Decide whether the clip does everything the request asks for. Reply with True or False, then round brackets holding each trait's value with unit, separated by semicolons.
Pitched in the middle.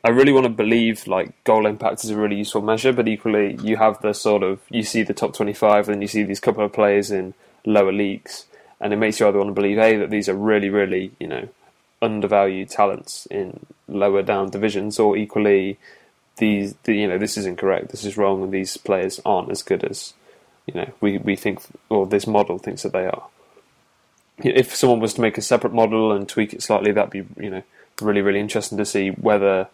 False (105 Hz)